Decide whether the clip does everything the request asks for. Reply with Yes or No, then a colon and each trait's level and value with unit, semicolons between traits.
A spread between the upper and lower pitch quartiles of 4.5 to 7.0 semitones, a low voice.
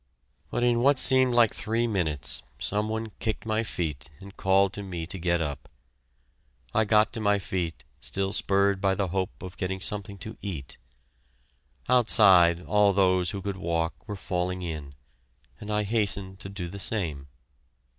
No: average, 3.0 semitones; very low, 95 Hz